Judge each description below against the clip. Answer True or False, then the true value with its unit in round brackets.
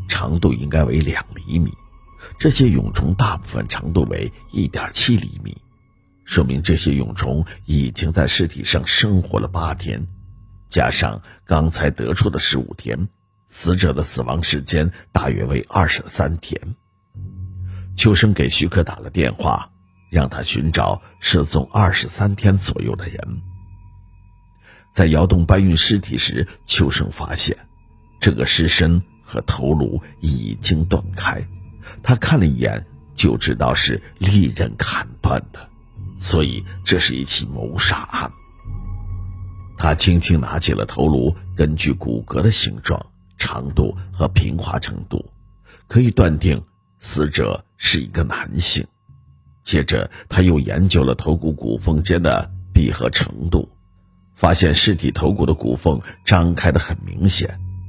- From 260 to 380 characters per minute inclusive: False (205 characters per minute)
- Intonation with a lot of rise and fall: False (3.5 semitones)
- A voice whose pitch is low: True (90 Hz)